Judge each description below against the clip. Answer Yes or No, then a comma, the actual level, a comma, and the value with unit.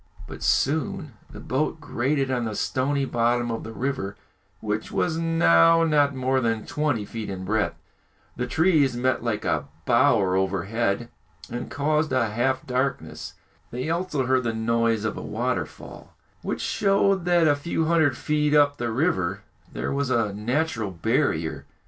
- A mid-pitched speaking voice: No, low, 130 Hz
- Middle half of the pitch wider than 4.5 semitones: Yes, average, 5.1 semitones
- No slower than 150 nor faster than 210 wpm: Yes, average, 155 wpm